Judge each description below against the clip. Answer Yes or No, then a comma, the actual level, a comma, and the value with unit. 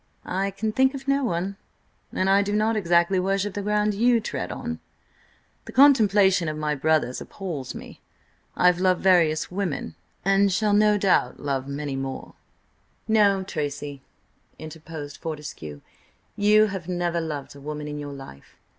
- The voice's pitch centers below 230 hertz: Yes, medium, 185 Hz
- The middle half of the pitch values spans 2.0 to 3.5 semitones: No, wide, 5.4 semitones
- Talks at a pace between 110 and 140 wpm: No, average, 155 wpm